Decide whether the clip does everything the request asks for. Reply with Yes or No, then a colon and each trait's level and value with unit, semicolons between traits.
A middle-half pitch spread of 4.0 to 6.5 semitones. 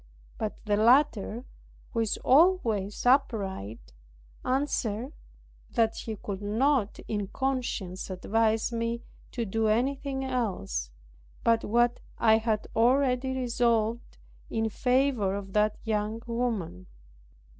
No: average, 3.3 semitones